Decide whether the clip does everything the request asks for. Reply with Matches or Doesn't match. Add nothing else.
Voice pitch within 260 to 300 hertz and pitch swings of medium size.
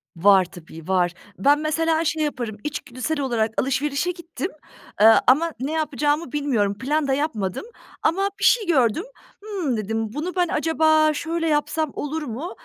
Doesn't match